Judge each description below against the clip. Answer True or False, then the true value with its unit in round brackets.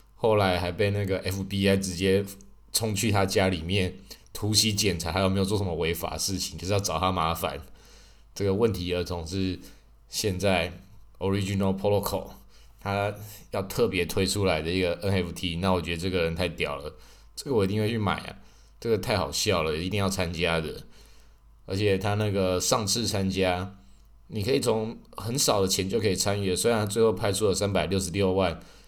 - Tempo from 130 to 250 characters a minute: False (300 characters per minute)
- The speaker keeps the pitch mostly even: True (1.9 semitones)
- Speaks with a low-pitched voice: True (95 Hz)